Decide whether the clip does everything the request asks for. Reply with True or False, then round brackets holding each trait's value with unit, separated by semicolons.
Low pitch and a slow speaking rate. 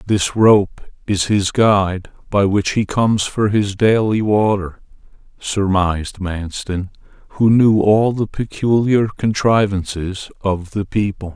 True (100 Hz; 125 wpm)